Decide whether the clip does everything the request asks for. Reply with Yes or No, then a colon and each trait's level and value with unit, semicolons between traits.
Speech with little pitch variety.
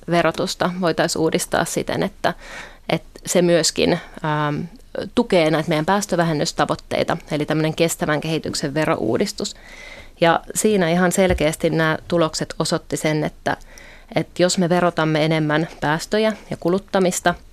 Yes: narrow, 2.3 semitones